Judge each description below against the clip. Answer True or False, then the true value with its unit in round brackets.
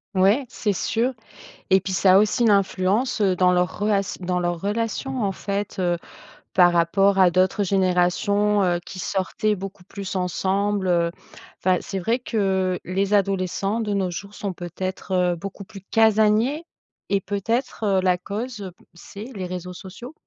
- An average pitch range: False (2.2 semitones)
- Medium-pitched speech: False (195 Hz)